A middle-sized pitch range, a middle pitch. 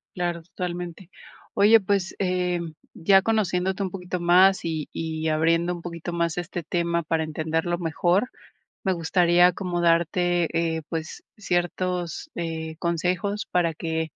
No: narrow, 1.6 semitones; medium, 175 Hz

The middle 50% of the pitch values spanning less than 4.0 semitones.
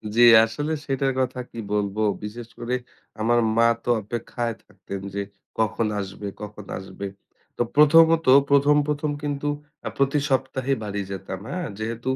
No: average, 5.0 semitones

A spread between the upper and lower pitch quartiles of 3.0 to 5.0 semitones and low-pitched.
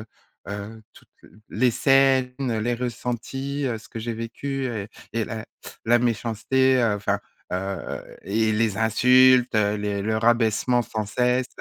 No: narrow, 2.6 semitones; low, 115 Hz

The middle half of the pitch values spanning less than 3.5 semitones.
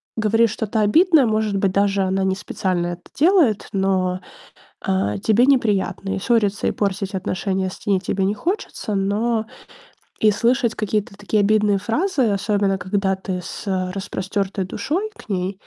Yes: narrow, 2.4 semitones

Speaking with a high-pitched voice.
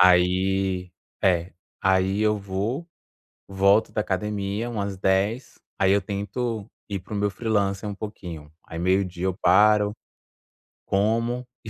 No: low, 100 Hz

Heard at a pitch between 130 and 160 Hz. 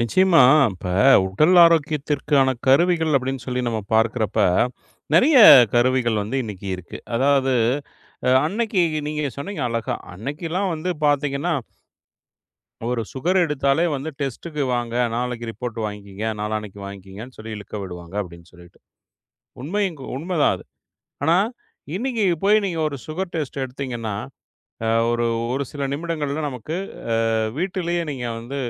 Yes: low, 135 Hz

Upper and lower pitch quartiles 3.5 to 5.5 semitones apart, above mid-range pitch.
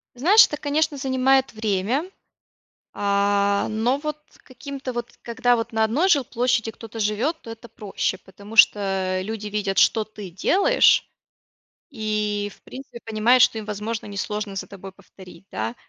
Yes: average, 4.1 semitones; high, 220 Hz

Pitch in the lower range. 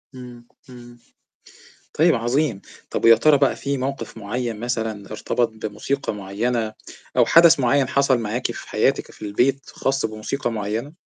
Yes: low, 120 Hz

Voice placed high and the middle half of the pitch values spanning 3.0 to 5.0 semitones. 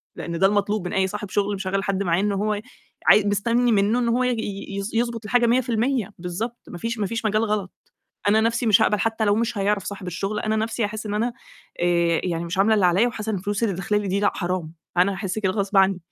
No: high, 205 Hz; narrow, 2.6 semitones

